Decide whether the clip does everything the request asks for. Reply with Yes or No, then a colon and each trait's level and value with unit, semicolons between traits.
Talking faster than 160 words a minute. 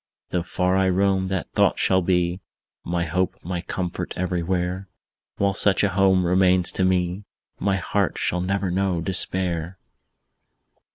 No: average, 145 wpm